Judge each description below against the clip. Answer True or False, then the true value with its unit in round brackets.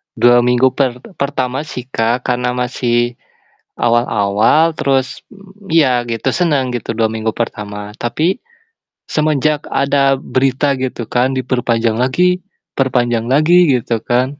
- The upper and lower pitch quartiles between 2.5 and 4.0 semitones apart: True (2.8 semitones)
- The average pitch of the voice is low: True (125 Hz)